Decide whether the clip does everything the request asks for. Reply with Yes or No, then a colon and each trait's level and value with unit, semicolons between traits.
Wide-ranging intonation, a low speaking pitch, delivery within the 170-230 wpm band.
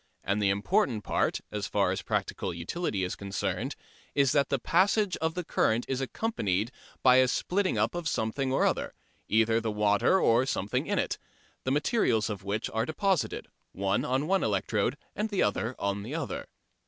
Yes: wide, 7.8 semitones; low, 125 Hz; average, 180 wpm